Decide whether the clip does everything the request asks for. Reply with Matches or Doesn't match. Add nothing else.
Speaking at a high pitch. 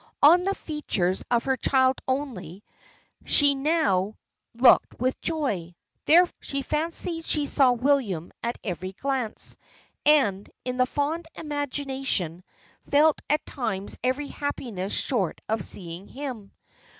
Matches